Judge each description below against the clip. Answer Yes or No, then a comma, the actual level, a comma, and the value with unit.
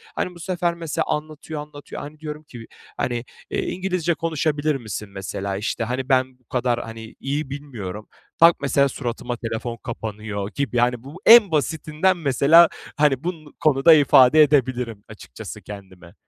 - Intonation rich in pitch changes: No, average, 4.8 semitones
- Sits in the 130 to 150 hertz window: Yes, medium, 140 Hz